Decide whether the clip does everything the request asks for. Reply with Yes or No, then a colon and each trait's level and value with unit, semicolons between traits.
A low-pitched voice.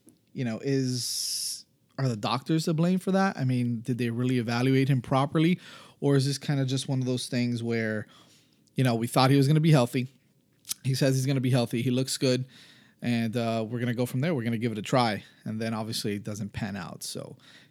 Yes: low, 125 Hz